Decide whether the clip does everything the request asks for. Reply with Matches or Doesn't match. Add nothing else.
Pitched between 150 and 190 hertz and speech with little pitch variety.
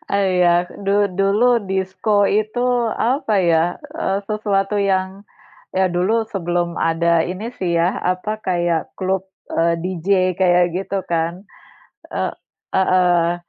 Matches